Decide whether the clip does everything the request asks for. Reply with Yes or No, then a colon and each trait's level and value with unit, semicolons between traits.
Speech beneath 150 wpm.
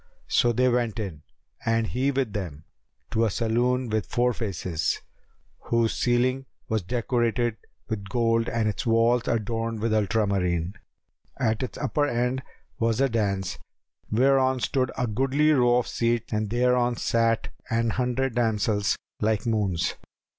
Yes: average, 140 wpm